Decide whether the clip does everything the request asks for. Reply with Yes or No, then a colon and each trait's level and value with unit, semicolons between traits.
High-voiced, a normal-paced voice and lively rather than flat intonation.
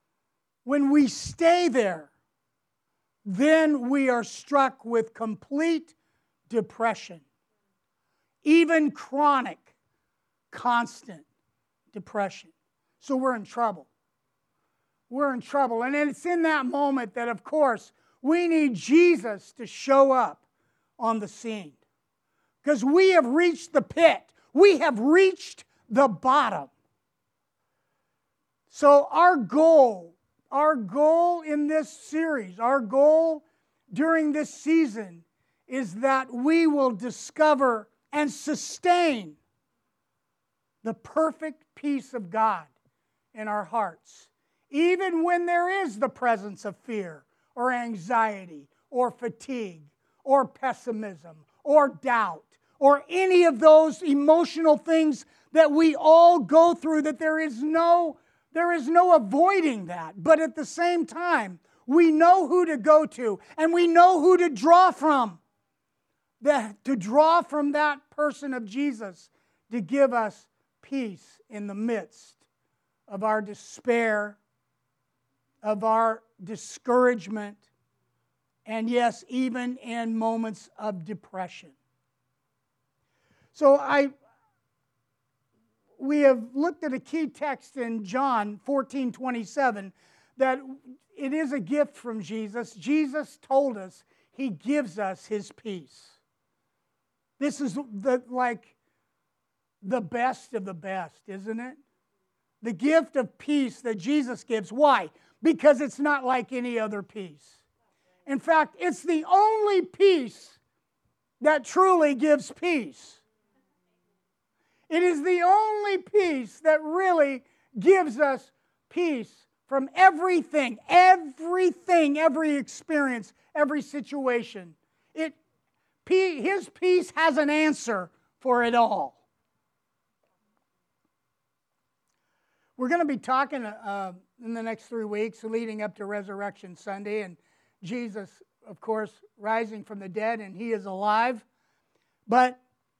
No: very high, 265 Hz; slow, 115 wpm; wide, 6.1 semitones